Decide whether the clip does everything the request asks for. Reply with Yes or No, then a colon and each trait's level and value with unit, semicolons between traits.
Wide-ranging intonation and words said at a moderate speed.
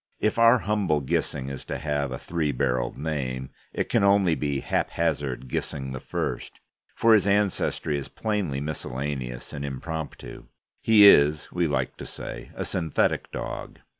Yes: wide, 6.0 semitones; average, 150 wpm